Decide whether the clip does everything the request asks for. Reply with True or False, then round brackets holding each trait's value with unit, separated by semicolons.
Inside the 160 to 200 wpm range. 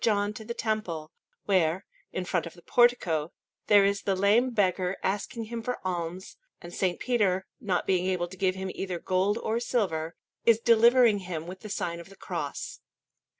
True (185 wpm)